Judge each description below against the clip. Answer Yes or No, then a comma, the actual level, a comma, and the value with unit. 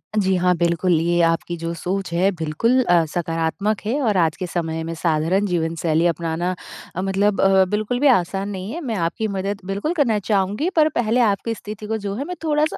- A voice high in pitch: Yes, high, 195 Hz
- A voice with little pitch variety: No, average, 4.2 semitones